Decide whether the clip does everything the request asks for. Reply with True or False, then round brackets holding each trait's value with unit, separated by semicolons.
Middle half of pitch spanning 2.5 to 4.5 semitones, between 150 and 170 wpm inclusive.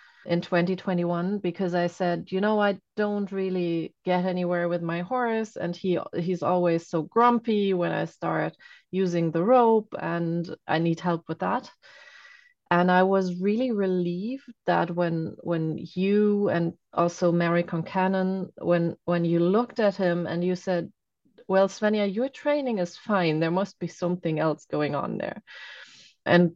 True (2.8 semitones; 160 wpm)